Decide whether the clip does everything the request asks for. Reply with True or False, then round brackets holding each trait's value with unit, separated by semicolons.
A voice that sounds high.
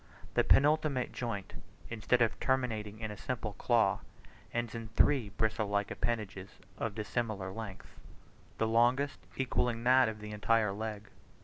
False (110 Hz)